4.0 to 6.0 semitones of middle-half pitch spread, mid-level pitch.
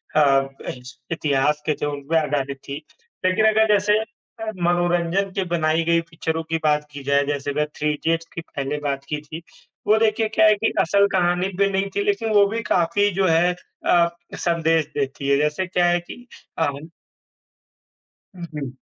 Yes: average, 4.5 semitones; medium, 165 Hz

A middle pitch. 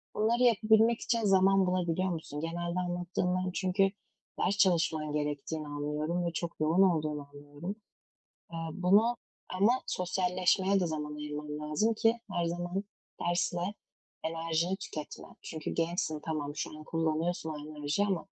Yes: medium, 175 Hz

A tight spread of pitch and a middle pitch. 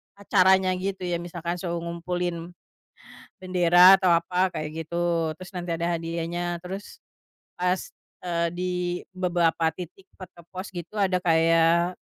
Yes: narrow, 1.5 semitones; medium, 175 Hz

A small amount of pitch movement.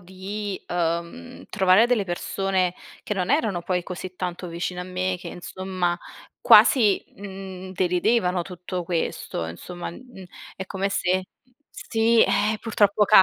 Yes: narrow, 2.3 semitones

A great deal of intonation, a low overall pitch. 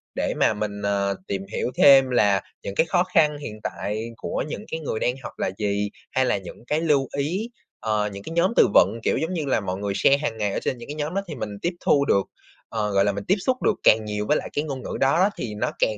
Yes: wide, 6.6 semitones; low, 120 Hz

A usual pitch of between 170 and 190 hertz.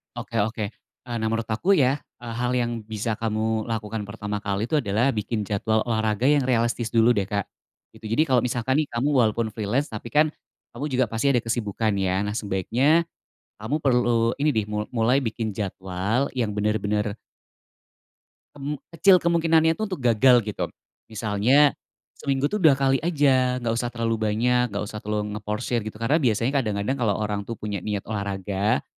No: low, 115 Hz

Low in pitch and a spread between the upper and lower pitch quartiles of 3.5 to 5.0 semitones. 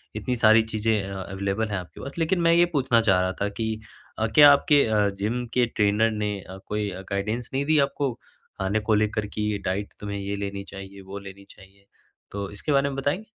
Yes: low, 105 Hz; average, 3.8 semitones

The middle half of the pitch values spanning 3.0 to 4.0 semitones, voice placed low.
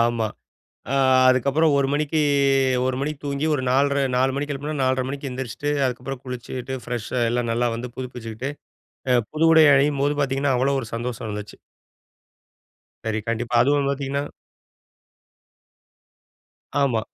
No: narrow, 2.5 semitones; low, 130 Hz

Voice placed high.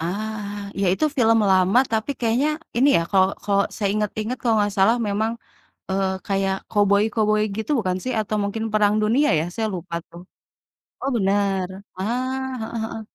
Yes: high, 210 Hz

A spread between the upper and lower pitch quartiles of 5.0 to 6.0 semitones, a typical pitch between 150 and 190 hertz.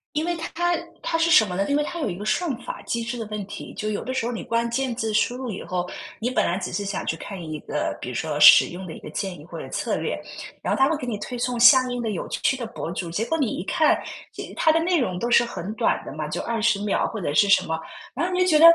No: wide, 5.6 semitones; high, 230 Hz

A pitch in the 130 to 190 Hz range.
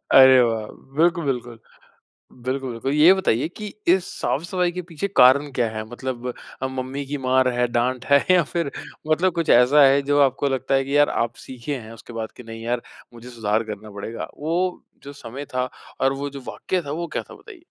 Yes: low, 135 Hz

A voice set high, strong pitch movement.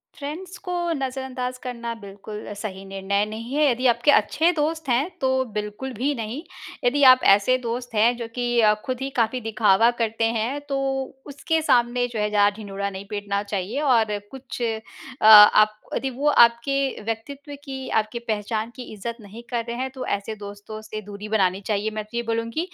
No: high, 230 Hz; average, 3.6 semitones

